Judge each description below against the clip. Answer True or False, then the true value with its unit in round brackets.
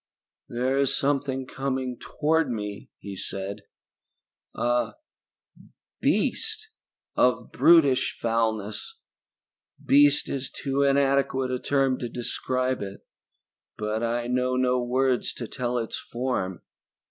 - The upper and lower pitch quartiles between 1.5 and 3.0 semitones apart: True (2.7 semitones)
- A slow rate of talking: True (110 wpm)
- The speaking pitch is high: False (130 Hz)